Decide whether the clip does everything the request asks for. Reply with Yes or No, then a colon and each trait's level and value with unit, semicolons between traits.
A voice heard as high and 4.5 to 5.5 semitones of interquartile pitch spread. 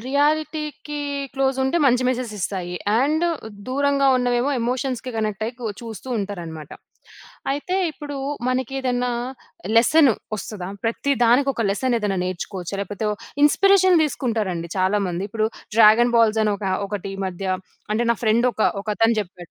Yes: high, 230 Hz; average, 4.9 semitones